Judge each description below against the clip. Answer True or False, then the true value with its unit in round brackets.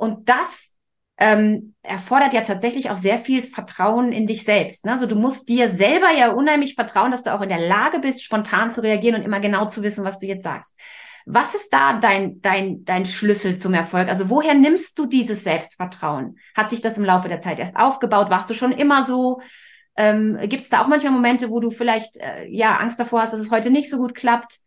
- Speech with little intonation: False (3.8 semitones)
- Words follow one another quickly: True (225 wpm)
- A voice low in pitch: False (225 Hz)